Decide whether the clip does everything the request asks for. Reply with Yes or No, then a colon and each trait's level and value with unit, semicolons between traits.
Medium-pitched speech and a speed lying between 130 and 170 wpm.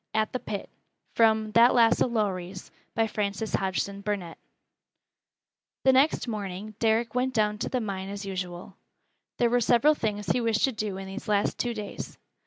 No: high, 215 Hz; average, 155 wpm